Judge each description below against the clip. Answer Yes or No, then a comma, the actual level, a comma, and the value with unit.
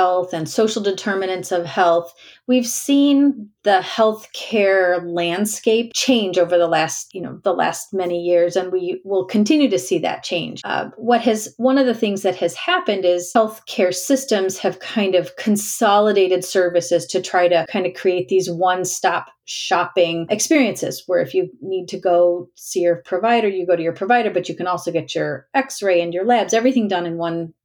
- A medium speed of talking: Yes, average, 190 wpm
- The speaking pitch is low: No, medium, 185 Hz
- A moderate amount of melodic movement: Yes, average, 3.8 semitones